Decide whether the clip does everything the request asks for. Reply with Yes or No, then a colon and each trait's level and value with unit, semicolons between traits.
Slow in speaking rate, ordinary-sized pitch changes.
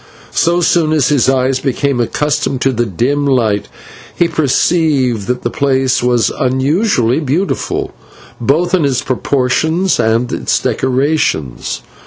Yes: slow, 130 wpm; average, 3.9 semitones